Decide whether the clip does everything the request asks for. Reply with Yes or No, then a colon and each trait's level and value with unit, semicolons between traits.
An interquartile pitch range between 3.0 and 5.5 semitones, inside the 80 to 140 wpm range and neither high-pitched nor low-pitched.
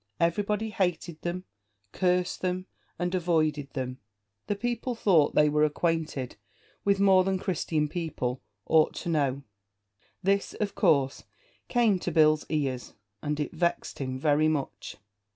Yes: average, 3.9 semitones; slow, 135 wpm; medium, 165 Hz